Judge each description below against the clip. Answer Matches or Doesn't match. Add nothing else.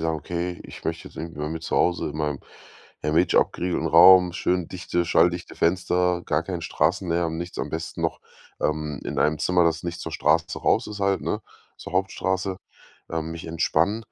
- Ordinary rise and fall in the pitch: Doesn't match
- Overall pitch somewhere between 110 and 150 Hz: Doesn't match